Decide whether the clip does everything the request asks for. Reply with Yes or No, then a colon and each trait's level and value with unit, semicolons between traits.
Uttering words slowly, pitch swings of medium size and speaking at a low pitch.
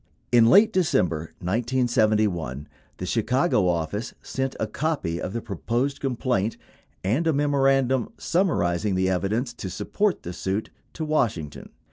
No: slow, 130 wpm; wide, 6.5 semitones; low, 115 Hz